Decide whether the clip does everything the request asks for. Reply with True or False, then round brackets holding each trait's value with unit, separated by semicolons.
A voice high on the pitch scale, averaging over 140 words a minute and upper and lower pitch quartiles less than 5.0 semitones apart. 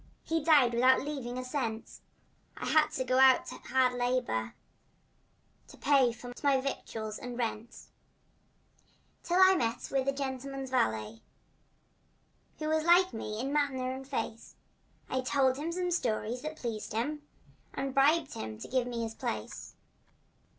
True (260 Hz; 155 wpm; 3.3 semitones)